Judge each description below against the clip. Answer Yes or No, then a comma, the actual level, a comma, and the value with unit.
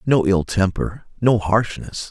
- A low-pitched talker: Yes, low, 105 Hz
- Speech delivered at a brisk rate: No, average, 140 wpm